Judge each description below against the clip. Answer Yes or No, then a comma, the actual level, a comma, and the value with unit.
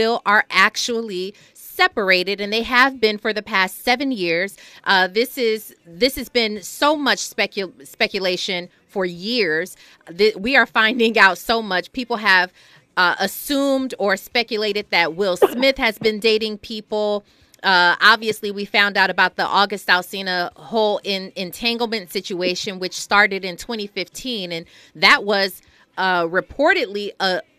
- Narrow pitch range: No, average, 3.7 semitones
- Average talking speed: Yes, average, 145 wpm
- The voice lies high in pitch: Yes, high, 205 Hz